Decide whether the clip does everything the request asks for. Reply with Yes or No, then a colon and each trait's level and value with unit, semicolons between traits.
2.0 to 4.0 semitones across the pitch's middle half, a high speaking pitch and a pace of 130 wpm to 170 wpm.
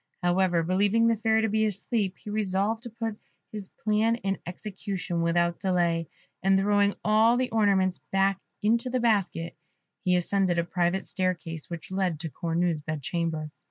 Yes: average, 3.7 semitones; high, 195 Hz; average, 160 wpm